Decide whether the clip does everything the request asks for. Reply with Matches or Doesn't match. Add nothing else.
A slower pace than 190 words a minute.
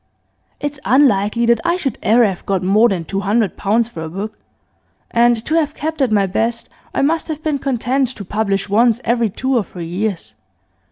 Doesn't match